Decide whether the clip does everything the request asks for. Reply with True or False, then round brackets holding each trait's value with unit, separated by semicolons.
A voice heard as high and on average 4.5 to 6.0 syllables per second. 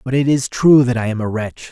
False (125 Hz; 5.6 syllables/s)